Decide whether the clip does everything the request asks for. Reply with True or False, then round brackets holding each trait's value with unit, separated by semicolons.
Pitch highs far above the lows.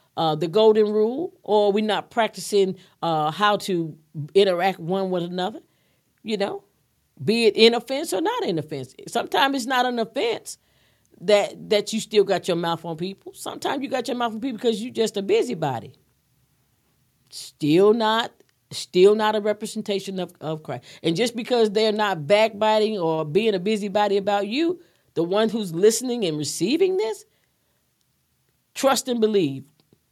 False (4.6 semitones)